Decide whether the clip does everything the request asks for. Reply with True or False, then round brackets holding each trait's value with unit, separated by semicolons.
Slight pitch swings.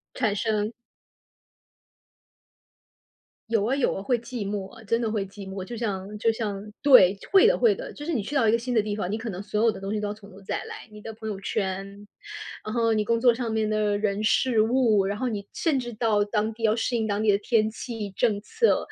True (2.2 semitones)